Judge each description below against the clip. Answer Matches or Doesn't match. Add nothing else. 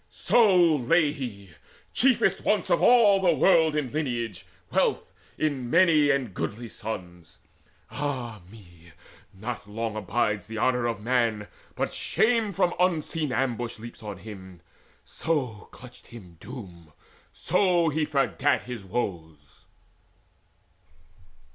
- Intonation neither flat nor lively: Doesn't match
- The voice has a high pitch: Doesn't match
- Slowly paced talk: Matches